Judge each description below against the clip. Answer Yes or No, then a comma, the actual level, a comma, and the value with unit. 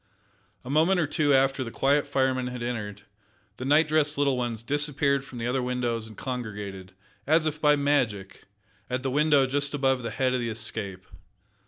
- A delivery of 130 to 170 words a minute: No, average, 185 wpm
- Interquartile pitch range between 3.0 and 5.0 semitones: Yes, average, 3.6 semitones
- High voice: No, low, 130 Hz